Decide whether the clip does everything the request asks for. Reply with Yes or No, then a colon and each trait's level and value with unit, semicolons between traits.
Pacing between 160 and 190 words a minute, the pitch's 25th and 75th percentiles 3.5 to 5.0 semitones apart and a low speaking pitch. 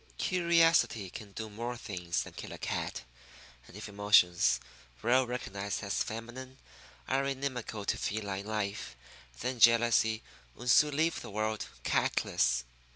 No: average, 140 wpm; average, 4.1 semitones; low, 110 Hz